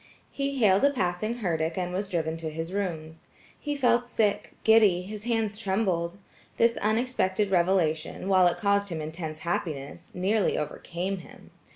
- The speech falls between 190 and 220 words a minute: No, average, 155 wpm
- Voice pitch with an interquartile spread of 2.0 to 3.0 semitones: No, average, 4.2 semitones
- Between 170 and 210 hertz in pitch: Yes, high, 190 Hz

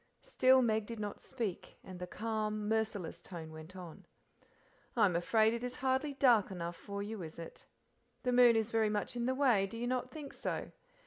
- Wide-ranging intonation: No, average, 4.2 semitones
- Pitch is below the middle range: No, high, 220 Hz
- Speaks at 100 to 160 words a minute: No, average, 200 wpm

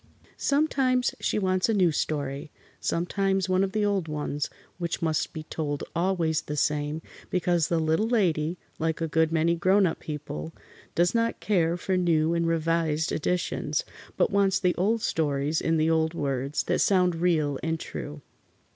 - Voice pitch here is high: No, medium, 165 Hz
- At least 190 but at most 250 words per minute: No, average, 165 wpm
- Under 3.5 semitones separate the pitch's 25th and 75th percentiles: Yes, average, 3.1 semitones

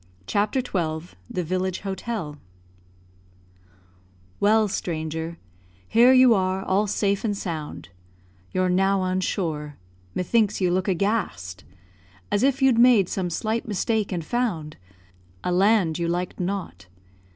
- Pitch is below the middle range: No, high, 190 Hz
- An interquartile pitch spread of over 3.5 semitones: Yes, average, 3.9 semitones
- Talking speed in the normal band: No, slow, 125 wpm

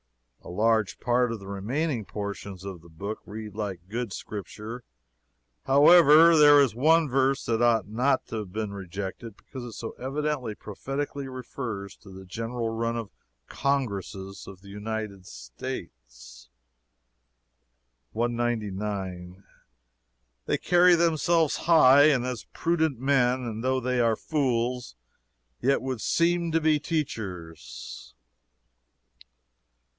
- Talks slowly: Yes, slow, 125 wpm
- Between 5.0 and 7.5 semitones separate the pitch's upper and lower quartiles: Yes, wide, 5.4 semitones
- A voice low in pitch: Yes, low, 115 Hz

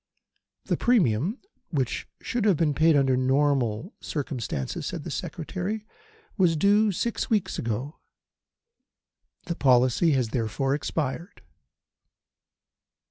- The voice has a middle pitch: Yes, medium, 145 Hz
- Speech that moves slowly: Yes, slow, 105 wpm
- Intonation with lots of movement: Yes, wide, 6.3 semitones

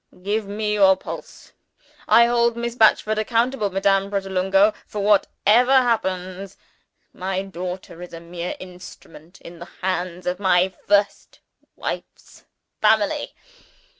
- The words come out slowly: Yes, slow, 120 wpm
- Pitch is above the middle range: Yes, high, 195 Hz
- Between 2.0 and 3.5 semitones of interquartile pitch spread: Yes, average, 2.8 semitones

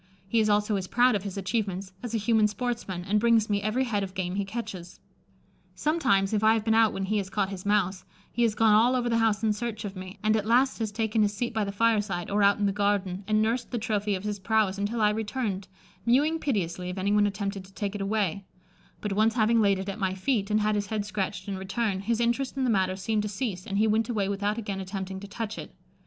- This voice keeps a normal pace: No, fast, 255 wpm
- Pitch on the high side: Yes, high, 210 Hz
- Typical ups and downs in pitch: No, narrow, 2.3 semitones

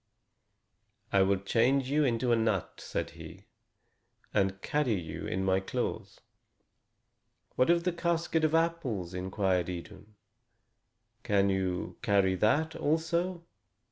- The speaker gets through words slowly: Yes, slow, 120 wpm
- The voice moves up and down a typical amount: No, wide, 8.8 semitones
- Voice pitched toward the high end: No, low, 110 Hz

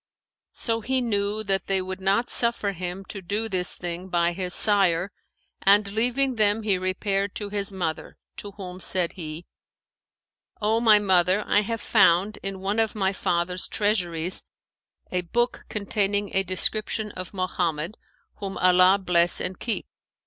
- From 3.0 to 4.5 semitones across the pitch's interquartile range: No, narrow, 2.5 semitones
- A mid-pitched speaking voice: No, high, 195 Hz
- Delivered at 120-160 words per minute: Yes, average, 155 wpm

